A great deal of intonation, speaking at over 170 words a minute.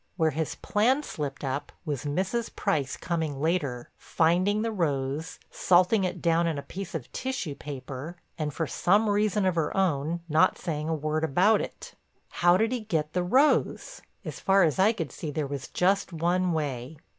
No: average, 4.5 semitones; average, 180 wpm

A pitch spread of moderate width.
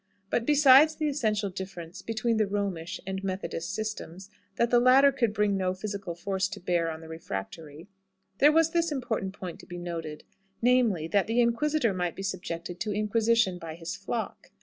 Yes: average, 4.9 semitones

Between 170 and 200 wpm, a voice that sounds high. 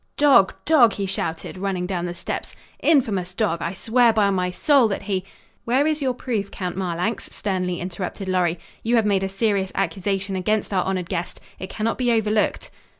Yes: average, 190 wpm; high, 195 Hz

